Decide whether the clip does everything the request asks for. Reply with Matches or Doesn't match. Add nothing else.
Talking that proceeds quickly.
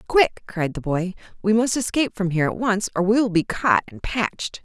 Matches